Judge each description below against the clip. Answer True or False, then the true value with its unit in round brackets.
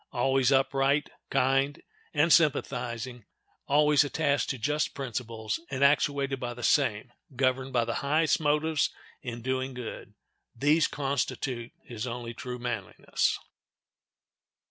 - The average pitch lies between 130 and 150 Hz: True (135 Hz)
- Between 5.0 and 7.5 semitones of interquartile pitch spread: False (2.8 semitones)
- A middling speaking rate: False (120 wpm)